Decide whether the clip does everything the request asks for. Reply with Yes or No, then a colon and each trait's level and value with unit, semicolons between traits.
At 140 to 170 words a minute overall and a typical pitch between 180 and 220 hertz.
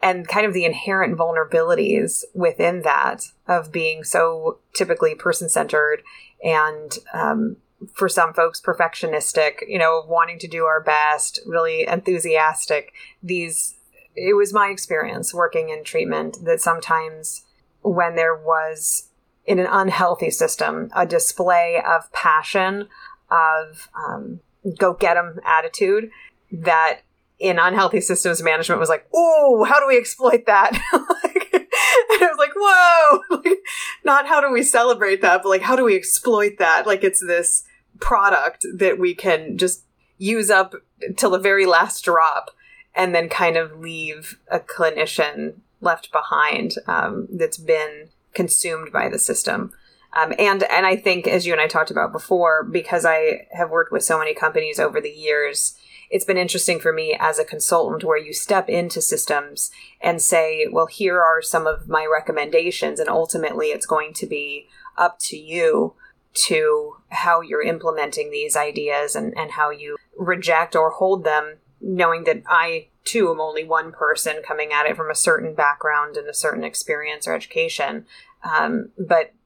Yes: average, 160 wpm; medium, 185 Hz